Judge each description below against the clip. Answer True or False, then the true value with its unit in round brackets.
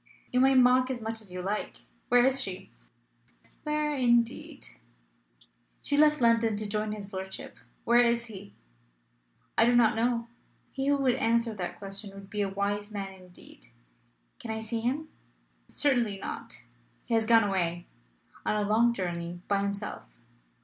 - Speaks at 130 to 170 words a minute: True (160 wpm)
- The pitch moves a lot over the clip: False (3.4 semitones)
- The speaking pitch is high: True (220 Hz)